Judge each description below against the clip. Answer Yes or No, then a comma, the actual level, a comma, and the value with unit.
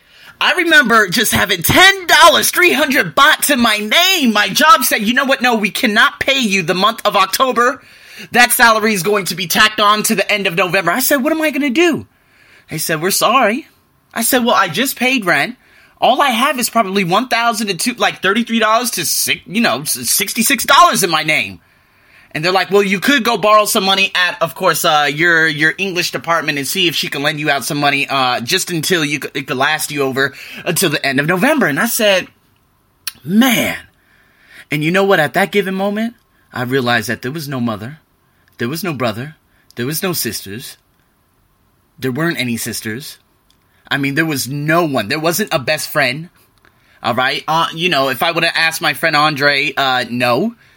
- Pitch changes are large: Yes, wide, 7.6 semitones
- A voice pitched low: No, high, 190 Hz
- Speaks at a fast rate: Yes, fast, 215 wpm